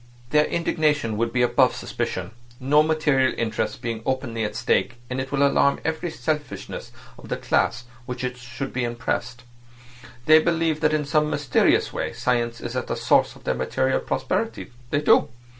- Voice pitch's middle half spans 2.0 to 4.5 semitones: Yes, average, 4.0 semitones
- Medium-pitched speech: No, low, 130 Hz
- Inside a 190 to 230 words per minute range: No, average, 170 wpm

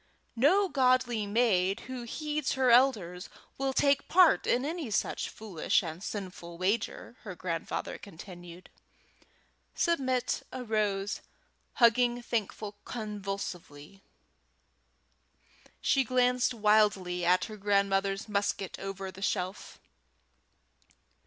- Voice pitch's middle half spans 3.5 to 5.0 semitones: Yes, average, 4.6 semitones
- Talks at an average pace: No, slow, 100 wpm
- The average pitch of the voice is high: Yes, high, 210 Hz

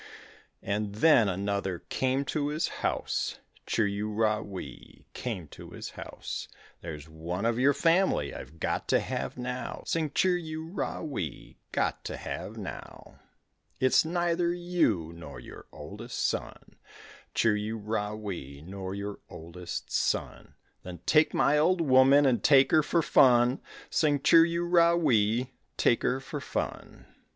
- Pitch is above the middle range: No, low, 120 Hz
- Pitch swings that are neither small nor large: No, wide, 7.6 semitones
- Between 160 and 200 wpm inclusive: No, average, 150 wpm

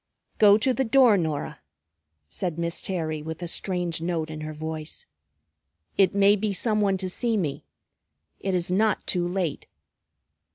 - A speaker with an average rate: Yes, average, 160 wpm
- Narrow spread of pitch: No, average, 4.2 semitones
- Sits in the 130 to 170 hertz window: No, medium, 180 Hz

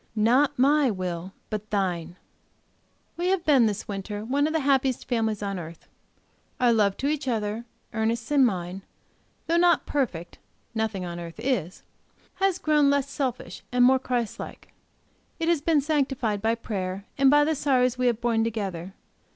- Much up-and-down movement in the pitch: Yes, wide, 5.8 semitones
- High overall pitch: Yes, high, 235 Hz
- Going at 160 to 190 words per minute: Yes, average, 165 wpm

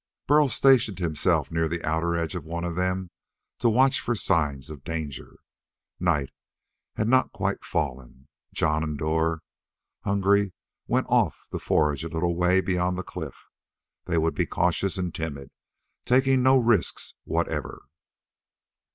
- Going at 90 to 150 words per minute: Yes, average, 145 wpm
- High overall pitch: No, very low, 85 Hz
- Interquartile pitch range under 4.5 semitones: Yes, average, 3.9 semitones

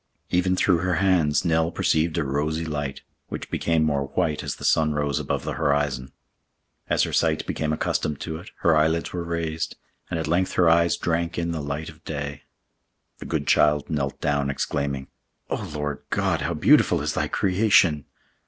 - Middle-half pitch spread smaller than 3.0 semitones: Yes, narrow, 2.4 semitones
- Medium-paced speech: Yes, average, 180 wpm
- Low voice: Yes, very low, 80 Hz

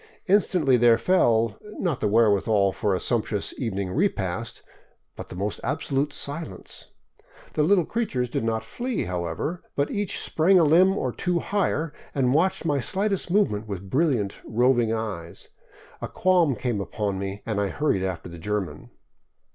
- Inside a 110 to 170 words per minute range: Yes, average, 155 wpm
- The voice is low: Yes, low, 120 Hz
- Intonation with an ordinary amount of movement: No, wide, 8.4 semitones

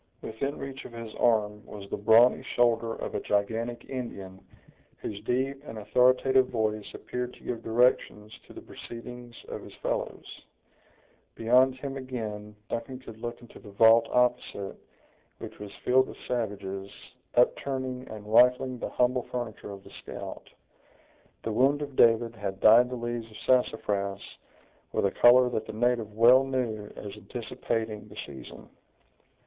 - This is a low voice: Yes, low, 115 Hz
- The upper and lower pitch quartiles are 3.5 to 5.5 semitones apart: No, average, 2.9 semitones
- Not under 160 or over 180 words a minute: No, average, 150 wpm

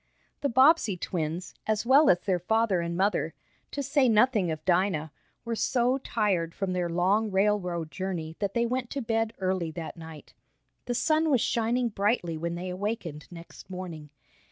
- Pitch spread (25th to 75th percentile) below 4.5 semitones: No, average, 5.2 semitones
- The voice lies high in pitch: Yes, high, 195 Hz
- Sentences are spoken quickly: No, average, 170 wpm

